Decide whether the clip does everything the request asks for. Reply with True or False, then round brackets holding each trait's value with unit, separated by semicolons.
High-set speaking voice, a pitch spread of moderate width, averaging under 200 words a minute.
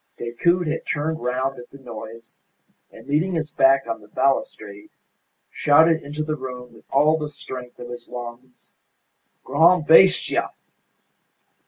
False (135 Hz; 4.1 semitones; 140 wpm)